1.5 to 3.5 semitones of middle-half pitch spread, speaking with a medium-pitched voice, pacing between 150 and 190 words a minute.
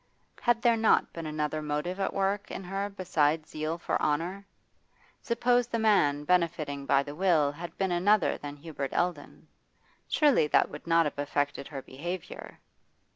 No: average, 4.8 semitones; medium, 165 Hz; average, 160 wpm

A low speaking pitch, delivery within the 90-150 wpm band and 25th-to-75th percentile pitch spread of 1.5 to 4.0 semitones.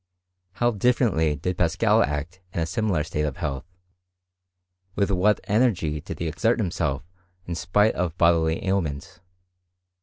No: very low, 85 Hz; average, 140 wpm; average, 4.7 semitones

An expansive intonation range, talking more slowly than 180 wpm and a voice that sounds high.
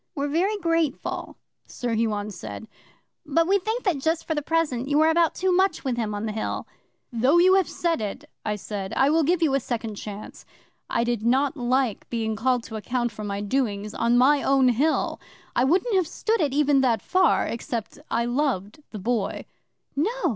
No: wide, 6.3 semitones; average, 200 wpm; very high, 260 Hz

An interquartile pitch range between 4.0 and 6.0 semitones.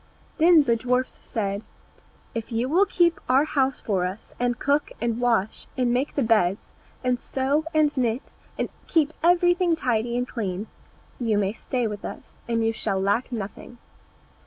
Yes: average, 4.3 semitones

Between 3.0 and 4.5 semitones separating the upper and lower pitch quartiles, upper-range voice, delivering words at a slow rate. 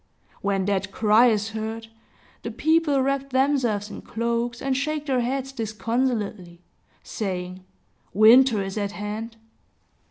Yes: average, 4.2 semitones; high, 225 Hz; slow, 125 wpm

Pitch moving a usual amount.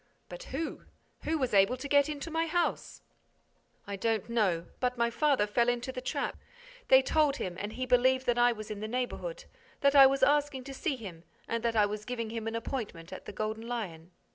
Yes: average, 4.2 semitones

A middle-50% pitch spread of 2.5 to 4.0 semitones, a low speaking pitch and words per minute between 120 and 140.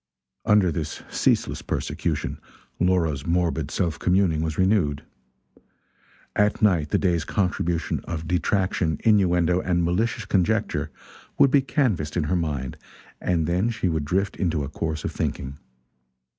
Yes: average, 3.3 semitones; very low, 85 Hz; slow, 135 wpm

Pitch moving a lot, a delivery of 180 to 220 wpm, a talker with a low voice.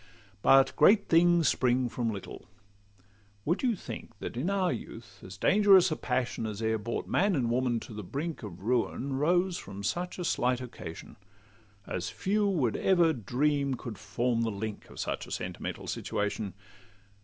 No: wide, 8.3 semitones; average, 165 wpm; low, 125 Hz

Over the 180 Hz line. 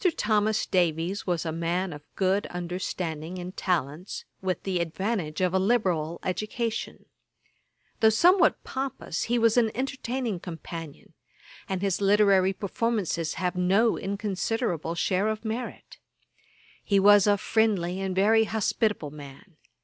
Yes: high, 190 Hz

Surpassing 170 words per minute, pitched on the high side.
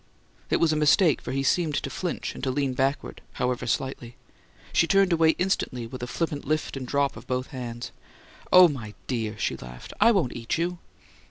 No: average, 195 wpm; low, 135 Hz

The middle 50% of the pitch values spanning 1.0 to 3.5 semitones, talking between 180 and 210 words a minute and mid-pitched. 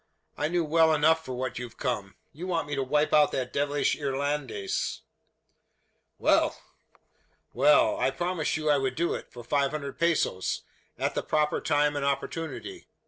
No: average, 2.8 semitones; average, 165 wpm; medium, 145 Hz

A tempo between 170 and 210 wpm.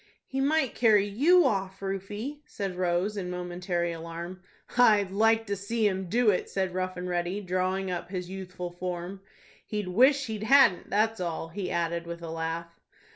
Yes: average, 175 wpm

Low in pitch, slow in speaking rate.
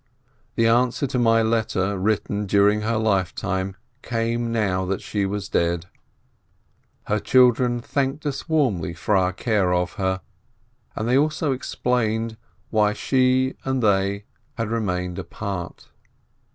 Yes: low, 110 Hz; slow, 130 wpm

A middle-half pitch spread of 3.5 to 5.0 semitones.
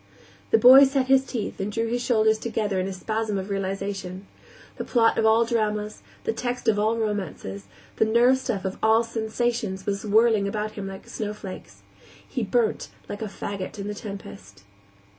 No: average, 2.7 semitones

